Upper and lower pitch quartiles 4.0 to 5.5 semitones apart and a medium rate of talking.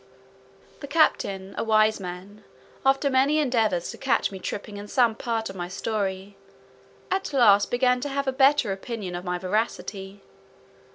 Yes: average, 5.2 semitones; average, 160 wpm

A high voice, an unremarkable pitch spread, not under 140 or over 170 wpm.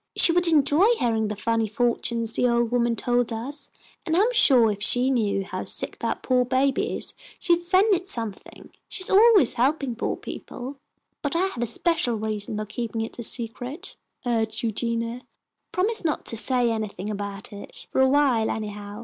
No: high, 240 Hz; average, 4.6 semitones; average, 180 wpm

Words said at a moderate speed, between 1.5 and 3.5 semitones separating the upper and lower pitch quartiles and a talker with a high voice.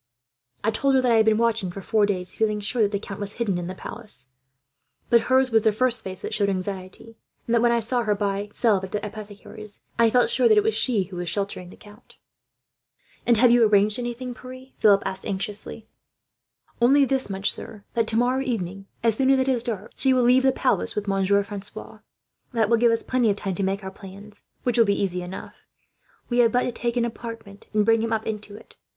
No: fast, 230 wpm; average, 3.2 semitones; high, 220 Hz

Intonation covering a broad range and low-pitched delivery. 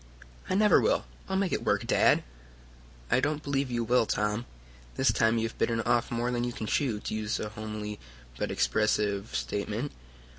No: average, 2.9 semitones; low, 115 Hz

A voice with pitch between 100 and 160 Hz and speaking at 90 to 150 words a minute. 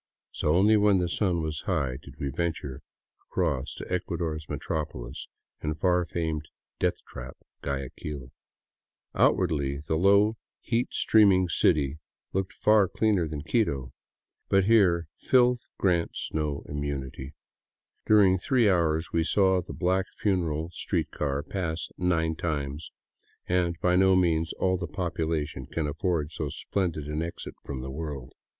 No: very low, 80 Hz; average, 140 wpm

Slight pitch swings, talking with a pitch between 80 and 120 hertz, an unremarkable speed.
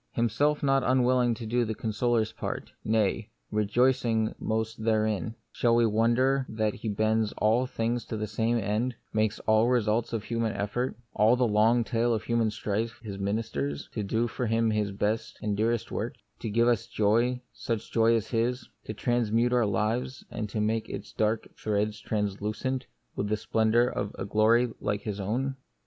Yes: narrow, 1.9 semitones; low, 110 Hz; average, 180 wpm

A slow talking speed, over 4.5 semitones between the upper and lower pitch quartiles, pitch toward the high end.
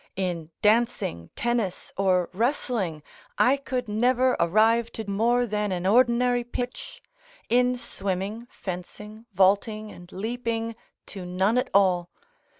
No: slow, 120 wpm; average, 4.2 semitones; high, 215 Hz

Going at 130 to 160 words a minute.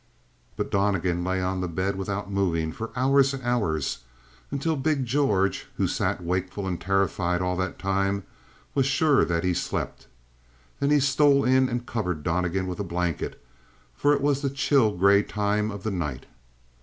No: average, 170 wpm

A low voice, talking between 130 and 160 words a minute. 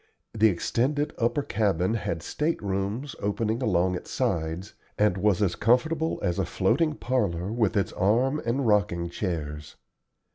Yes: low, 105 Hz; average, 145 wpm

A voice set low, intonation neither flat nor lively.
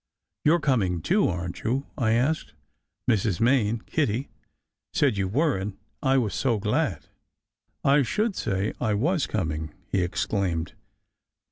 No: low, 110 Hz; wide, 6.2 semitones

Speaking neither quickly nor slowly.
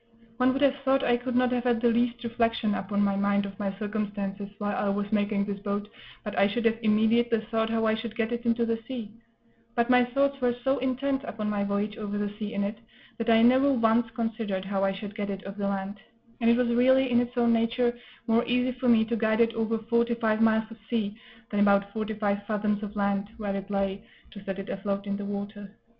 No: fast, 240 wpm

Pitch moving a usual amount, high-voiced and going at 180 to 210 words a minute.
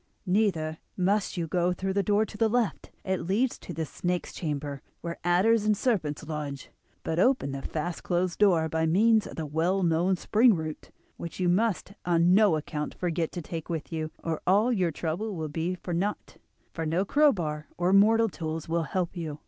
No: average, 3.9 semitones; medium, 175 Hz; average, 195 wpm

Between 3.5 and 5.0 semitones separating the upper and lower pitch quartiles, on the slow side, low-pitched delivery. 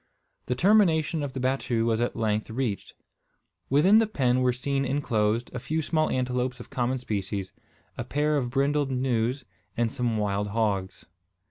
No: average, 3.8 semitones; average, 160 wpm; low, 125 Hz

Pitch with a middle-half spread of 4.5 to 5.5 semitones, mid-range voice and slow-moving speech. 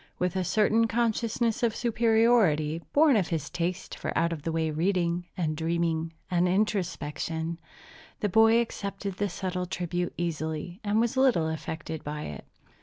No: average, 5.0 semitones; medium, 180 Hz; average, 155 wpm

